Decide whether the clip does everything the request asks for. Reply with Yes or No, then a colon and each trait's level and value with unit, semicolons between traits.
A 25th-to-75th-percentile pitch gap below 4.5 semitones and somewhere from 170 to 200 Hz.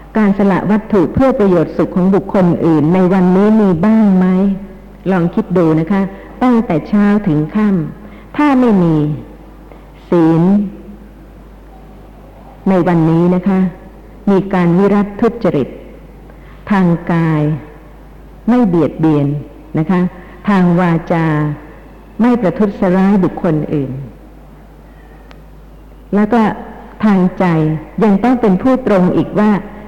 Yes: average, 3.8 semitones; medium, 185 Hz